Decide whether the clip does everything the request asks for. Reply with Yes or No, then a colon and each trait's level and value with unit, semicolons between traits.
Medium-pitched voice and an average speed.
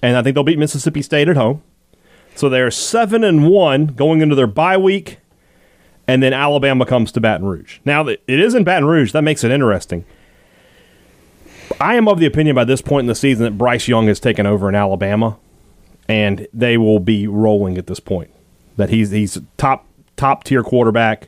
No: low, 125 Hz; average, 195 wpm